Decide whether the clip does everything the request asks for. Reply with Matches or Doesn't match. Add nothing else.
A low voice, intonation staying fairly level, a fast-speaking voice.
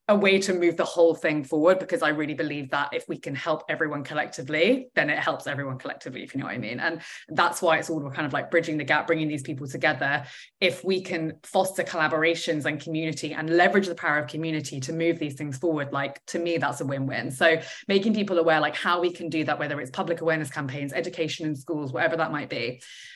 Doesn't match